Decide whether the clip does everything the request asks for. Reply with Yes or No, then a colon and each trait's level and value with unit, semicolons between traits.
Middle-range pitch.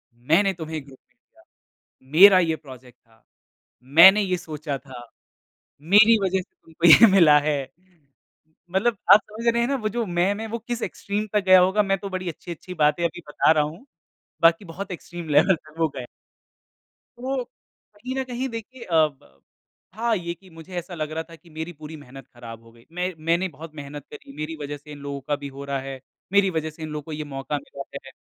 Yes: medium, 165 Hz